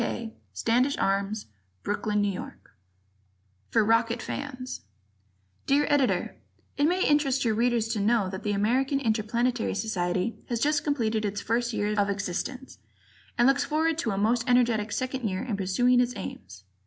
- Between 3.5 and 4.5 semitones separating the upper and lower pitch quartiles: Yes, average, 3.8 semitones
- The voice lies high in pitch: Yes, high, 230 Hz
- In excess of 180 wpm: No, average, 155 wpm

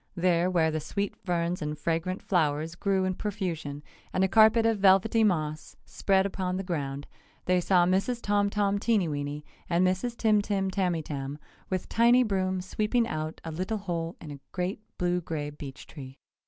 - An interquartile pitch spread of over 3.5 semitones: Yes, average, 3.9 semitones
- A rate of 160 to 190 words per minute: Yes, average, 170 wpm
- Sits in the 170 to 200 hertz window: Yes, medium, 185 Hz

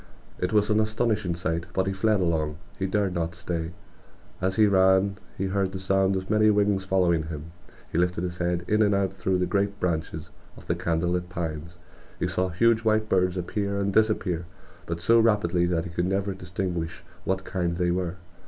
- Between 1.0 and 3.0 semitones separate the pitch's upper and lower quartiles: Yes, narrow, 2.5 semitones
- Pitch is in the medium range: No, very low, 95 Hz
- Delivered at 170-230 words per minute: Yes, average, 200 wpm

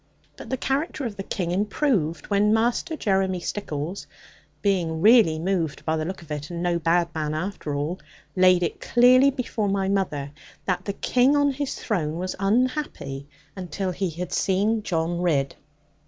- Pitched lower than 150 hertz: No, medium, 185 Hz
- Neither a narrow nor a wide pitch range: Yes, average, 4.7 semitones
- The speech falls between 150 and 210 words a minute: Yes, average, 170 wpm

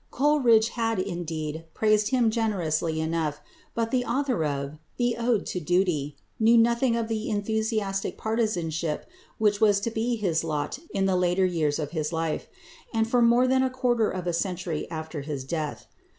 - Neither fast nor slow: Yes, average, 170 wpm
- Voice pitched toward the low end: No, high, 200 Hz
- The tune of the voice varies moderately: No, wide, 6.0 semitones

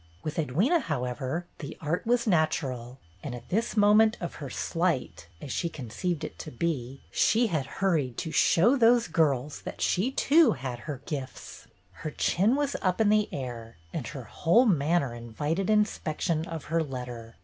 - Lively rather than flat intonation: Yes, wide, 7.7 semitones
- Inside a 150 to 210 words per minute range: Yes, average, 180 wpm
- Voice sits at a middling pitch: Yes, medium, 160 Hz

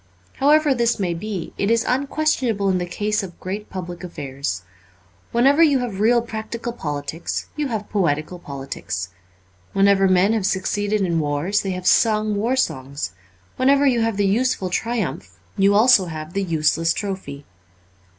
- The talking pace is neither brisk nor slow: Yes, average, 160 wpm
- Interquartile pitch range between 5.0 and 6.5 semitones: Yes, wide, 5.5 semitones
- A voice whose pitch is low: No, high, 200 Hz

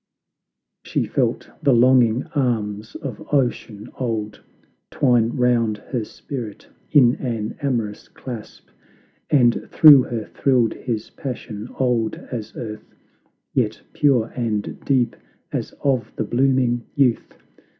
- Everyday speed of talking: No, slow, 115 wpm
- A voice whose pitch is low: Yes, low, 120 Hz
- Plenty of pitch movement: No, average, 2.8 semitones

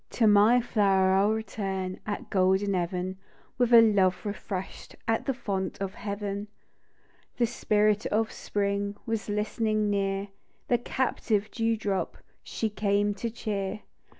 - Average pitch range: No, narrow, 2.0 semitones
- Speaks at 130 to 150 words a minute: Yes, average, 140 wpm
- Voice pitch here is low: No, high, 205 Hz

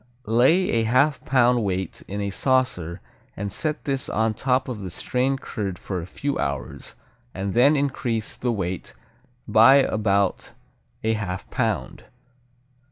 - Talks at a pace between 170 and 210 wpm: No, average, 145 wpm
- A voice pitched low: Yes, low, 110 Hz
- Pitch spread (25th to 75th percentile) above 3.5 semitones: Yes, average, 5.1 semitones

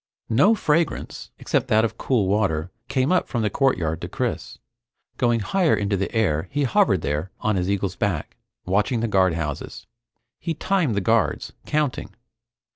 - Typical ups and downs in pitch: No, wide, 6.2 semitones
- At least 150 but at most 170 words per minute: Yes, average, 160 wpm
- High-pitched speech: No, low, 110 Hz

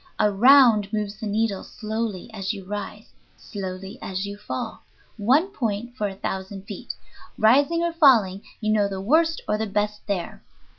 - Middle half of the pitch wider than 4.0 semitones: No, average, 3.1 semitones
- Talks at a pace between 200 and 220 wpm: No, average, 160 wpm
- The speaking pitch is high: Yes, high, 210 Hz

